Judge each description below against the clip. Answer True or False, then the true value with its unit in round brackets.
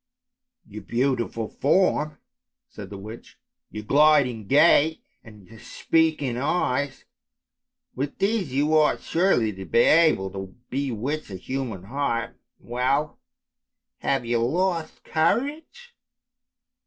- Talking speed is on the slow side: True (120 wpm)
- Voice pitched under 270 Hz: True (135 Hz)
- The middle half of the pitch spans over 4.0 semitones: True (5.6 semitones)